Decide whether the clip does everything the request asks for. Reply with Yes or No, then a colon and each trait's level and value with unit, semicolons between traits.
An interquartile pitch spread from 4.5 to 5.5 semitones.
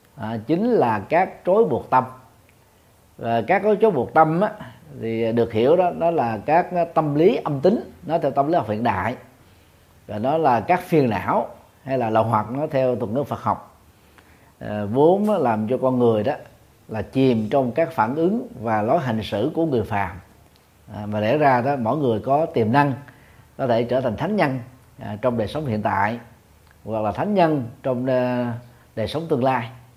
Yes: average, 5.2 semitones